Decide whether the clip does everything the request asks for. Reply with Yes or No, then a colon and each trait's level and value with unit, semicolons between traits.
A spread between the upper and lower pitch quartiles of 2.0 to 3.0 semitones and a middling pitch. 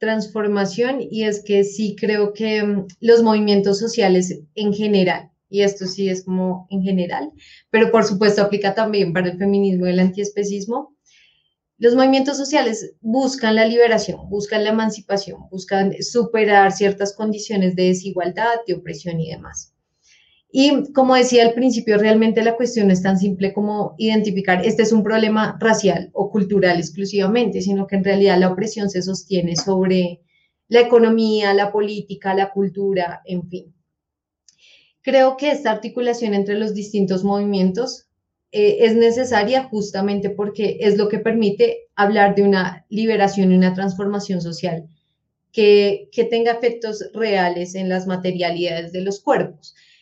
No: average, 2.7 semitones; high, 205 Hz